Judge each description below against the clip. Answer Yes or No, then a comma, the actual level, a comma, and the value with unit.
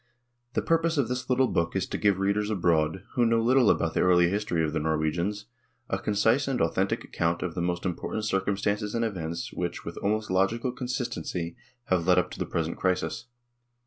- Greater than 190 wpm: Yes, fast, 205 wpm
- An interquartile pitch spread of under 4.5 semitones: No, average, 4.8 semitones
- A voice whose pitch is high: No, very low, 95 Hz